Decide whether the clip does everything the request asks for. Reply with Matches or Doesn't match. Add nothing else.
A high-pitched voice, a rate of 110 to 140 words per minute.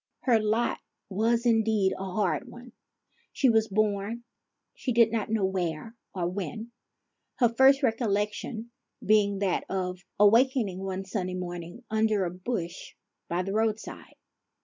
Matches